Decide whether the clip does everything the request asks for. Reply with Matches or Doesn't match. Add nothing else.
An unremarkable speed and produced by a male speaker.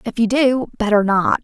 Doesn't match